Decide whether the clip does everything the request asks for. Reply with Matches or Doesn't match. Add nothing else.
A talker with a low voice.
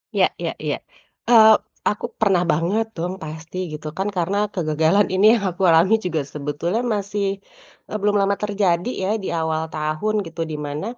Doesn't match